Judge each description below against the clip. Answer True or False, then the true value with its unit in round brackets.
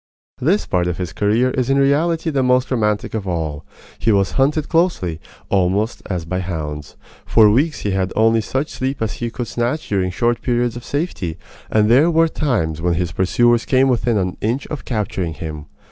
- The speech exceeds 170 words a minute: True (190 wpm)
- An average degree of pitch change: False (6.4 semitones)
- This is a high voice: False (110 Hz)